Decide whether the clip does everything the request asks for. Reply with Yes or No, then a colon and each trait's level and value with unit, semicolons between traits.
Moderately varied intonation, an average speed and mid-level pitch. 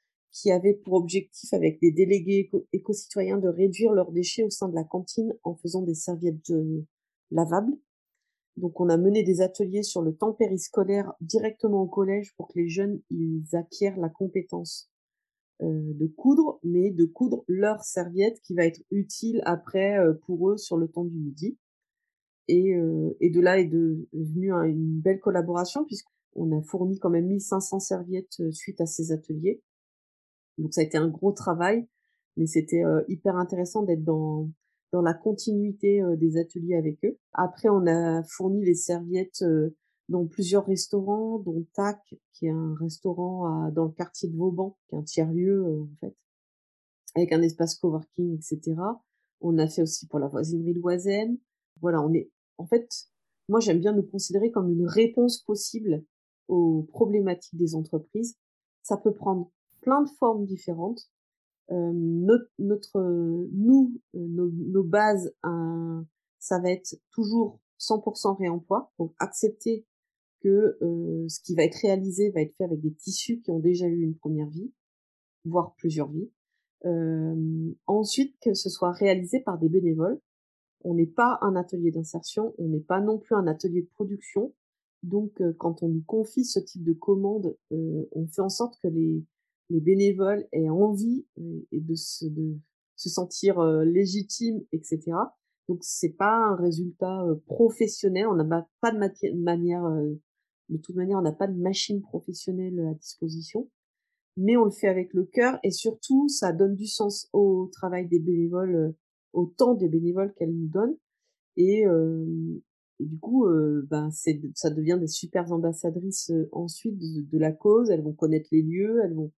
Yes: average, 3.6 semitones; average, 175 wpm; medium, 180 Hz